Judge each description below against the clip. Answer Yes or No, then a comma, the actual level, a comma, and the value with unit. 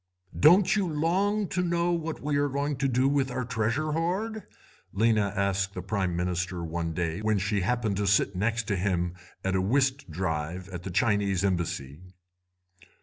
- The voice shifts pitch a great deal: Yes, wide, 7.7 semitones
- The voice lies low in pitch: Yes, low, 105 Hz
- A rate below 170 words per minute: No, average, 175 wpm